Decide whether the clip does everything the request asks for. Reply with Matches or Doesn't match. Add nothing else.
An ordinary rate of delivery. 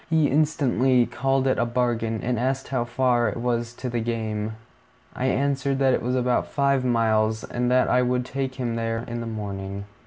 Matches